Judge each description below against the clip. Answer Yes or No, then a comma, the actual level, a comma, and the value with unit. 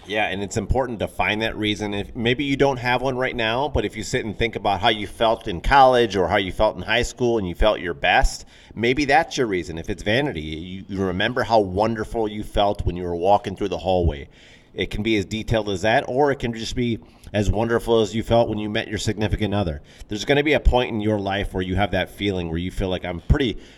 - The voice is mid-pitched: No, low, 105 Hz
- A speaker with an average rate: No, fast, 260 wpm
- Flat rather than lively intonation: No, average, 3.3 semitones